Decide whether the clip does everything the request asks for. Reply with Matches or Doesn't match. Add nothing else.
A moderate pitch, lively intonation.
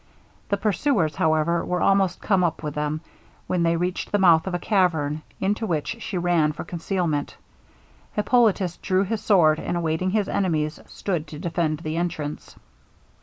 Doesn't match